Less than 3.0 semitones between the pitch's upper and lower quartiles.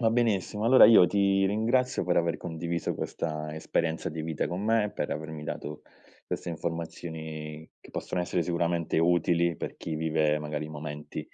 No: average, 3.7 semitones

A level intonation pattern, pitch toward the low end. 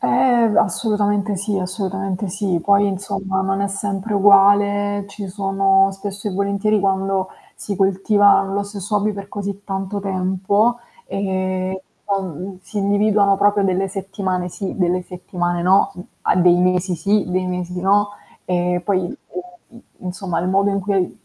No: narrow, 1.5 semitones; high, 195 Hz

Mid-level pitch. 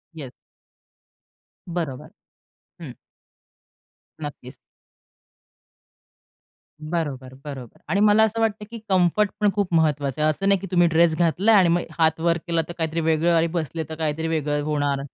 Yes: medium, 165 Hz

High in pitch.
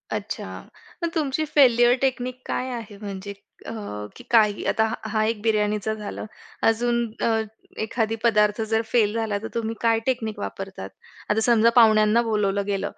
Yes: high, 220 Hz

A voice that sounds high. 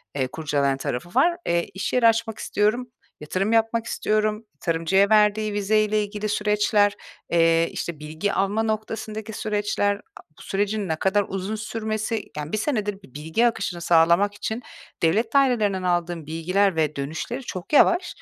Yes: high, 205 Hz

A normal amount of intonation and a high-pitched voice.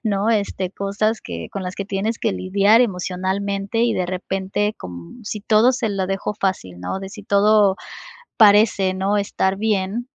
No: narrow, 2.1 semitones; high, 200 Hz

